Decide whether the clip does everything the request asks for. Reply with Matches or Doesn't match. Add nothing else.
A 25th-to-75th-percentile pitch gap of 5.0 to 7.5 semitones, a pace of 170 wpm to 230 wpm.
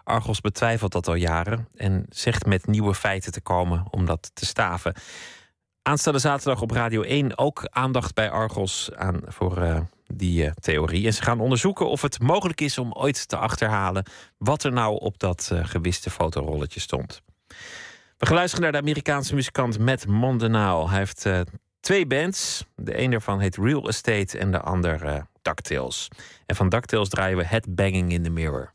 Matches